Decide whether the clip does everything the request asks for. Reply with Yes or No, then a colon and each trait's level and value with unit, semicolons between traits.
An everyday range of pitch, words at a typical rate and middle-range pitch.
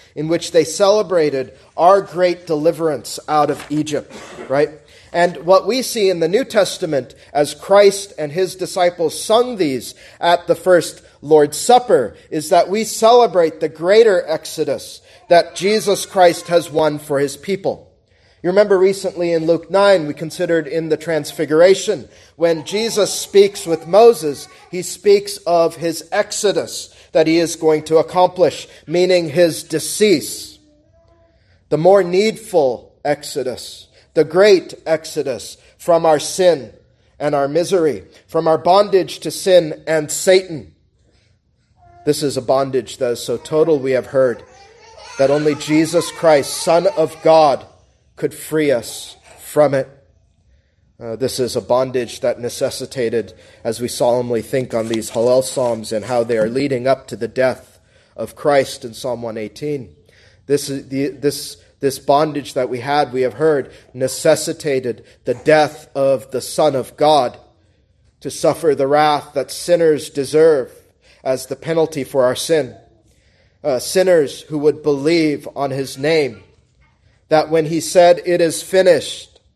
Yes: average, 4.9 semitones; average, 145 wpm; medium, 155 Hz